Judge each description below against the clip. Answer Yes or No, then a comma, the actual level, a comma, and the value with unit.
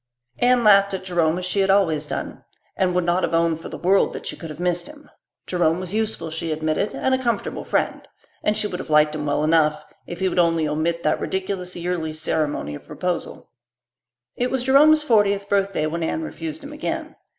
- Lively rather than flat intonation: No, average, 4.3 semitones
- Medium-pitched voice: Yes, medium, 180 Hz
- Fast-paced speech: Yes, fast, 210 wpm